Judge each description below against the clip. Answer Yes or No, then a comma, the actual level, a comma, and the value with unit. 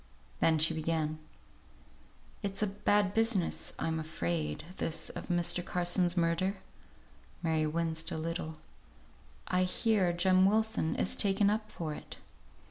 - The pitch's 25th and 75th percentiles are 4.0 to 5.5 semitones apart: No, average, 3.4 semitones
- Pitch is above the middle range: No, medium, 175 Hz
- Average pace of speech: No, slow, 125 wpm